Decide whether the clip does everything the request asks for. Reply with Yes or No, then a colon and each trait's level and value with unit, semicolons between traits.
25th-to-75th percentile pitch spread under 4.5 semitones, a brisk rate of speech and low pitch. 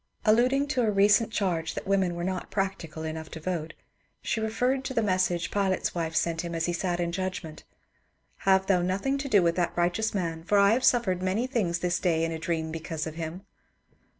No: average, 3.8 semitones; fast, 220 wpm; medium, 185 Hz